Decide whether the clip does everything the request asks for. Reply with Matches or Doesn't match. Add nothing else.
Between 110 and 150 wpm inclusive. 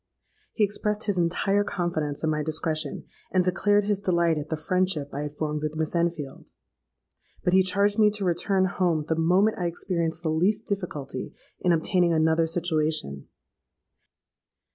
Doesn't match